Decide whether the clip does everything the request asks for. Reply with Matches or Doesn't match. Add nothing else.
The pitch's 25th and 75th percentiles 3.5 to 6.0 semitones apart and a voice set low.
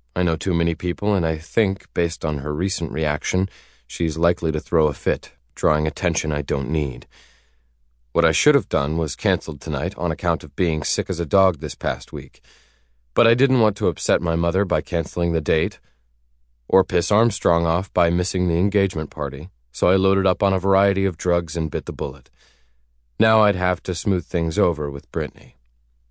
Matches